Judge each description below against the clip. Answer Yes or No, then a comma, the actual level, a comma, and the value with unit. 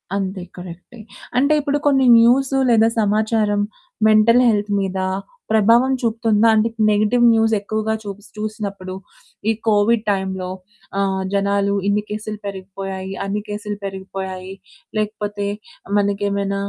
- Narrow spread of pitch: Yes, narrow, 2.0 semitones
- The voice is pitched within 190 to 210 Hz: Yes, high, 205 Hz